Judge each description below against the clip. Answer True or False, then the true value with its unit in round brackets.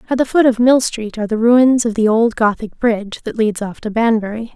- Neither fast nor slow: False (250 wpm)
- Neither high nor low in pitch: False (225 Hz)